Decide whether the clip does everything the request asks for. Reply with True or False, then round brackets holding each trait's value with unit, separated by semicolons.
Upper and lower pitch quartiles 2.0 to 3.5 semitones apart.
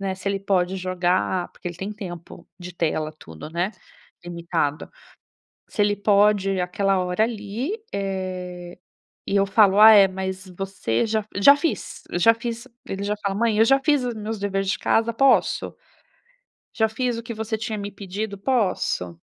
True (3.1 semitones)